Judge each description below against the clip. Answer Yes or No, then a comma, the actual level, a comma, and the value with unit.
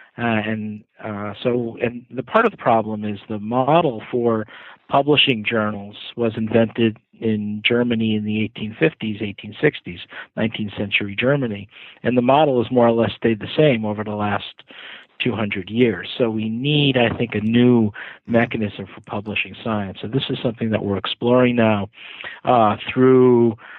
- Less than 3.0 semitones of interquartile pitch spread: Yes, narrow, 2.6 semitones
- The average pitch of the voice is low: Yes, low, 115 Hz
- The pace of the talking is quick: No, average, 160 wpm